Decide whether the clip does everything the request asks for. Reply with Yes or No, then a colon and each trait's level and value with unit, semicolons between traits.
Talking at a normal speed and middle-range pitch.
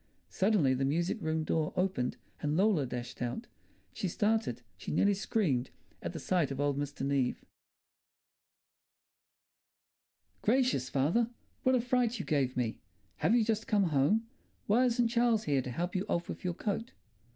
Yes: average, 160 wpm; medium, 175 Hz